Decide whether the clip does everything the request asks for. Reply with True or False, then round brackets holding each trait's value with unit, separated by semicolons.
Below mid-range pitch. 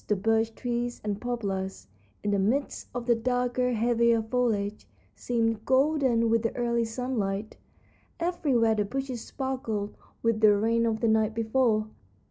False (230 Hz)